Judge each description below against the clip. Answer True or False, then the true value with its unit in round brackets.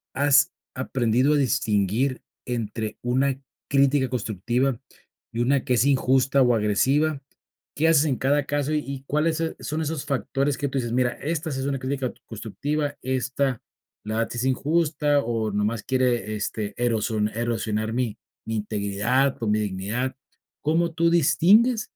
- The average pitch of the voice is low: True (130 Hz)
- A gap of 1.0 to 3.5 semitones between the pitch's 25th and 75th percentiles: False (4.0 semitones)